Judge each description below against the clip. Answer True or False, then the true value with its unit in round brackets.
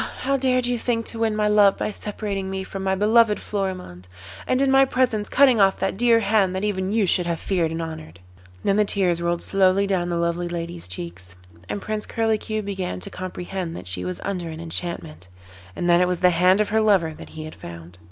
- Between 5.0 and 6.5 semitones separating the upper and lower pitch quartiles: False (3.8 semitones)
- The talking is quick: True (225 wpm)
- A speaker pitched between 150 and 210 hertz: True (190 Hz)